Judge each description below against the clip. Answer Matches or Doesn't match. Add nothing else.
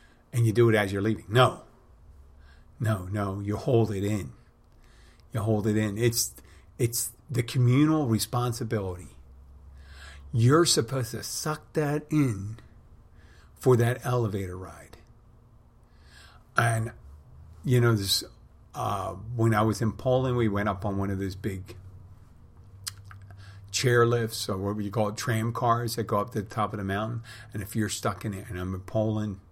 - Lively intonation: Doesn't match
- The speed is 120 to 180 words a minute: Matches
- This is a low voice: Matches